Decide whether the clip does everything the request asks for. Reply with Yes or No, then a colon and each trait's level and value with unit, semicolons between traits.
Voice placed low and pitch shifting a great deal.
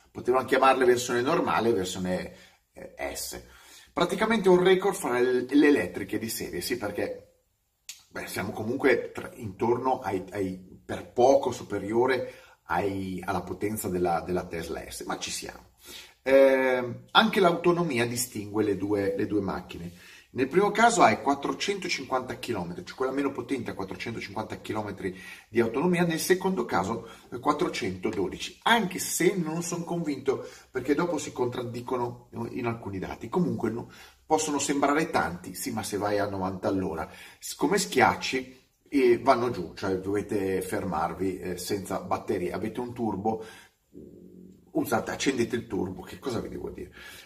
Yes: low, 120 Hz; wide, 6.9 semitones